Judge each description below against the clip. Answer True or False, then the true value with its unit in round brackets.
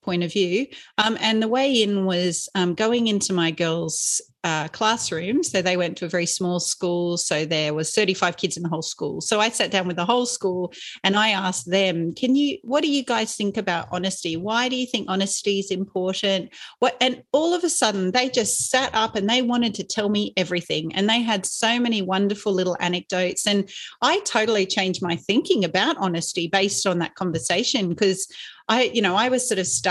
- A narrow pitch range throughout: False (4.0 semitones)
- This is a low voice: False (195 Hz)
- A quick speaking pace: True (215 wpm)